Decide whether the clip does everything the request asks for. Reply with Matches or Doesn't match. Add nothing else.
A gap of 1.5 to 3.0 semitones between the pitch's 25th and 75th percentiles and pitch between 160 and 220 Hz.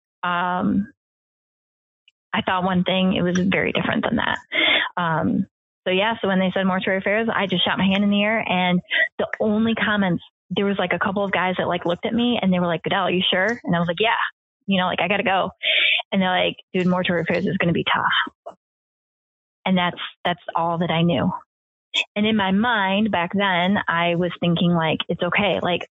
Matches